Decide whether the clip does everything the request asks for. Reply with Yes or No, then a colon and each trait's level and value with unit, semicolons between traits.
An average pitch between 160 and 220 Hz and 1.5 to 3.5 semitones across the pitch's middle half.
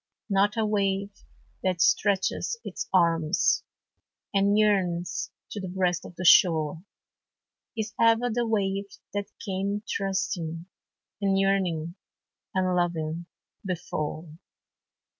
Yes: high, 190 Hz; average, 2.8 semitones